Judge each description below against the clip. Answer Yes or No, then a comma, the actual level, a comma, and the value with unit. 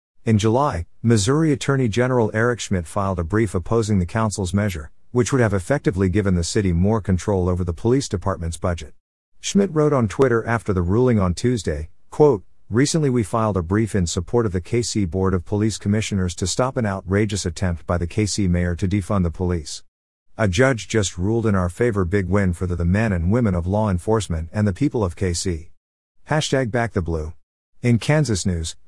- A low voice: Yes, low, 100 Hz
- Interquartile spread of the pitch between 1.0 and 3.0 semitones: No, average, 4.3 semitones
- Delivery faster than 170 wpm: Yes, average, 195 wpm